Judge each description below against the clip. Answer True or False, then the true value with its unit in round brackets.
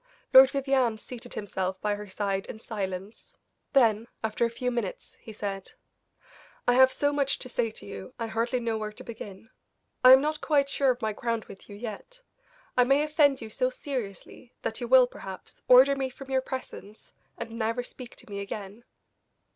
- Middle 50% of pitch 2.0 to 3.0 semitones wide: False (3.7 semitones)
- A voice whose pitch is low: False (235 Hz)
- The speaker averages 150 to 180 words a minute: False (190 wpm)